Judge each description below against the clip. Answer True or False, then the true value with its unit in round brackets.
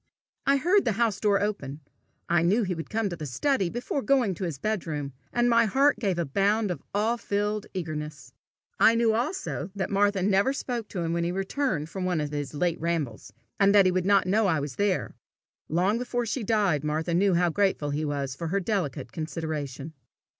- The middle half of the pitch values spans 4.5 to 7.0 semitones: True (5.3 semitones)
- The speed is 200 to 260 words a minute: True (205 wpm)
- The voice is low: False (190 Hz)